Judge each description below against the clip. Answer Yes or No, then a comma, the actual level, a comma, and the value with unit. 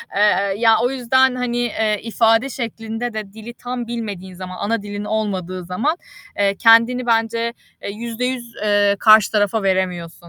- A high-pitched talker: Yes, high, 225 Hz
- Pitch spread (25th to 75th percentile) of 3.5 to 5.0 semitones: No, average, 2.8 semitones